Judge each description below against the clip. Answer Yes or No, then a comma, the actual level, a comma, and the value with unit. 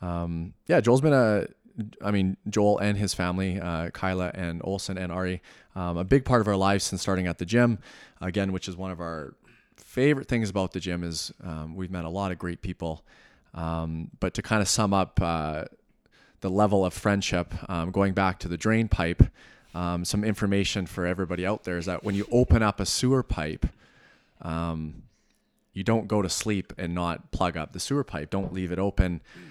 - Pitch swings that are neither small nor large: Yes, average, 3.0 semitones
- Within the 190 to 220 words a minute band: Yes, average, 200 wpm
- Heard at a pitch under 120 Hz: Yes, very low, 95 Hz